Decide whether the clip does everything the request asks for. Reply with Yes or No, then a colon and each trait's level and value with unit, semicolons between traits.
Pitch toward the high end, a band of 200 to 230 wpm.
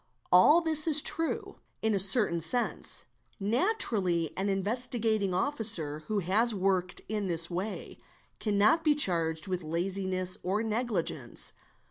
No: high, 200 Hz; average, 140 wpm